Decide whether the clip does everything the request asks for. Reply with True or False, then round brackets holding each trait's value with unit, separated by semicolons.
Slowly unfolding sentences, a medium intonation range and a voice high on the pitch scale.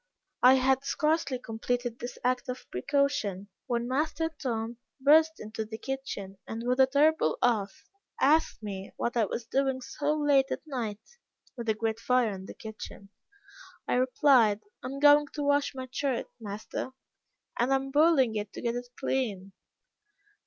False (160 wpm; 4.0 semitones; 250 Hz)